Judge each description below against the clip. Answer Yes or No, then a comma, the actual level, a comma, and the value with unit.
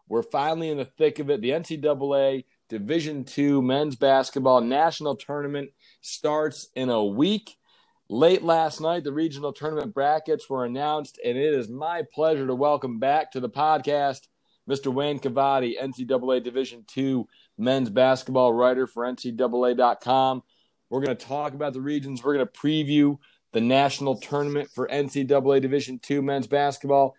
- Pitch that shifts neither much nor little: No, narrow, 2.3 semitones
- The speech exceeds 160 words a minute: No, average, 155 wpm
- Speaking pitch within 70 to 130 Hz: No, medium, 140 Hz